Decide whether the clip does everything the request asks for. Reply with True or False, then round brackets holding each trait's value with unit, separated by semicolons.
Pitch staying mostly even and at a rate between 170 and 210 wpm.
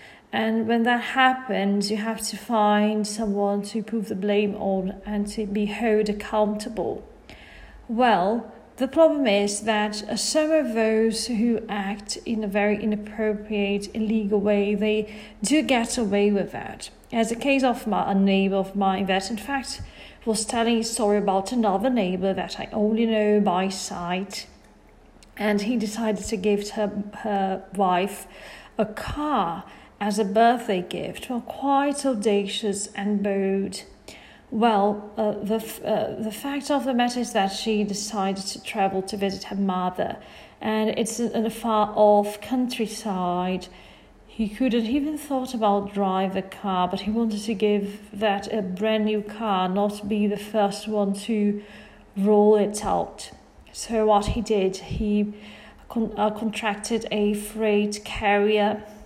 False (1.7 semitones; 150 wpm)